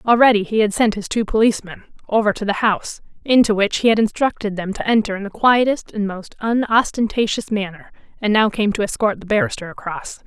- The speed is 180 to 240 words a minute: Yes, average, 200 wpm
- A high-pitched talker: Yes, high, 210 Hz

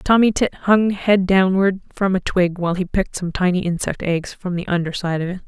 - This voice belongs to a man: No, female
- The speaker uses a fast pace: Yes, fast, 230 wpm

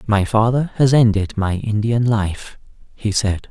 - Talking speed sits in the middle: Yes, average, 155 wpm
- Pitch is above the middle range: No, low, 110 Hz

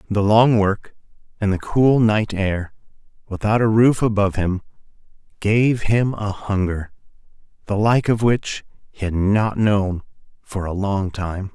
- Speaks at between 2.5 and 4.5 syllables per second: Yes, 4.0 syllables/s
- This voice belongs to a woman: No, male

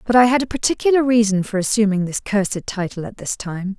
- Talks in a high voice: Yes, high, 215 Hz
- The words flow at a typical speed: No, fast, 220 wpm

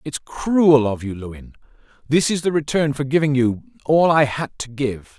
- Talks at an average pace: Yes, average, 185 wpm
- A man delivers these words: Yes, male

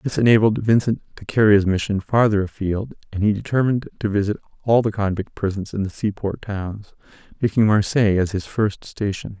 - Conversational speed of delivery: Yes, average, 180 wpm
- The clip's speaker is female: No, male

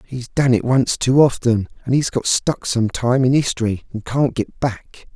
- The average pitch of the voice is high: No, low, 125 Hz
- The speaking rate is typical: No, fast, 210 wpm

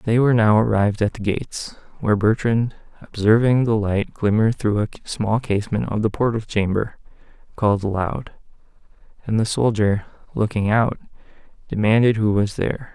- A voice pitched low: Yes, low, 110 Hz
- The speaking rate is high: No, average, 150 wpm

